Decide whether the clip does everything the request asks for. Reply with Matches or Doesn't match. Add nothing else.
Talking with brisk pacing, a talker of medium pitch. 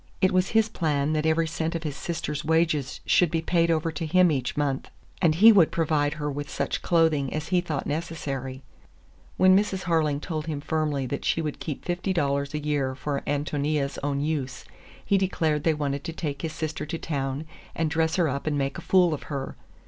Matches